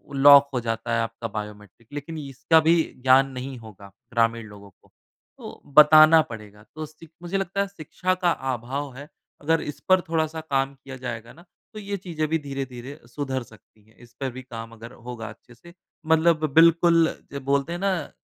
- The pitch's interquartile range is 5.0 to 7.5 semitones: Yes, wide, 5.6 semitones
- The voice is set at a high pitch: No, medium, 140 Hz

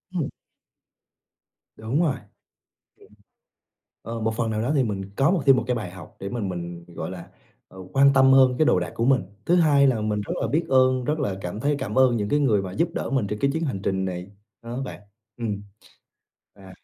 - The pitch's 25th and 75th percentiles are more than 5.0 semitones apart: Yes, wide, 5.5 semitones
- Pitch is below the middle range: Yes, low, 120 Hz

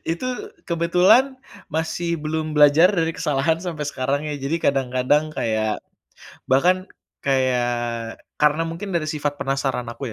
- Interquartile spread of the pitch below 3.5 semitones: No, average, 3.9 semitones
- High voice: No, medium, 150 Hz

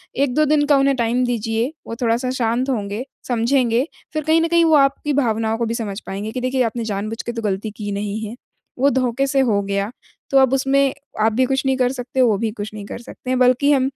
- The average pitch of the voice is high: Yes, high, 245 Hz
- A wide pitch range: No, average, 3.3 semitones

